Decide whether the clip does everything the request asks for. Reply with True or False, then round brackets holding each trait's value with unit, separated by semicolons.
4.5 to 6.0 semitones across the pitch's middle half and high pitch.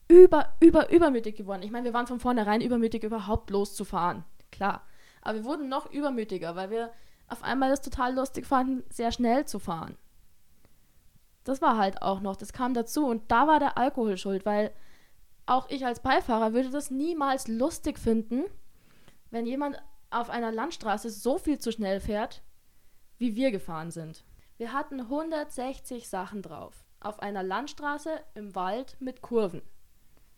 True (4.8 semitones; 240 Hz)